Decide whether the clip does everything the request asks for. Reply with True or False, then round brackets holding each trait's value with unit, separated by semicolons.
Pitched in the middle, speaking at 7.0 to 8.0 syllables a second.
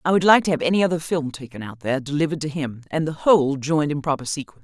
True (150 Hz; 7.4 syllables/s)